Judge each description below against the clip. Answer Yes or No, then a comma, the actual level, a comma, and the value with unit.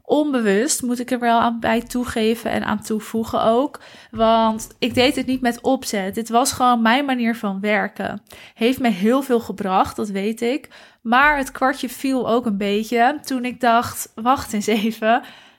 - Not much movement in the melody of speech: Yes, narrow, 2.2 semitones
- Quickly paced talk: No, average, 180 wpm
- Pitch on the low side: No, high, 235 Hz